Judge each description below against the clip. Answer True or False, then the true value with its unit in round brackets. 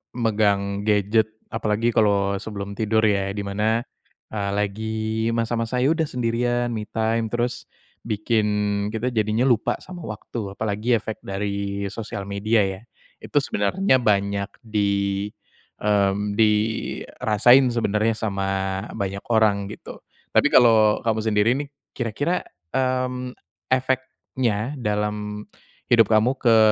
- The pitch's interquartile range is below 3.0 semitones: True (2.4 semitones)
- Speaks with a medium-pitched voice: False (110 Hz)